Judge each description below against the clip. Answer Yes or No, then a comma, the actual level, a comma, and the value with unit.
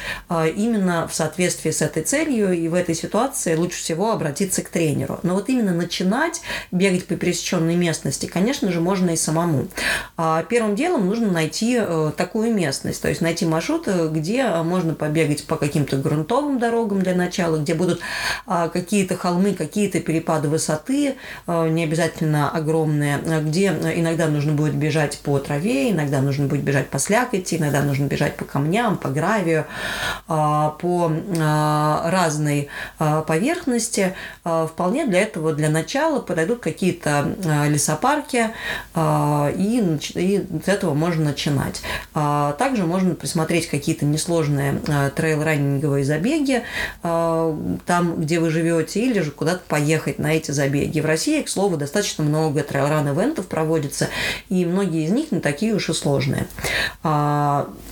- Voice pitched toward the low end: No, medium, 165 Hz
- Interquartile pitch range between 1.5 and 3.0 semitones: No, average, 3.7 semitones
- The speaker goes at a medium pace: Yes, average, 135 wpm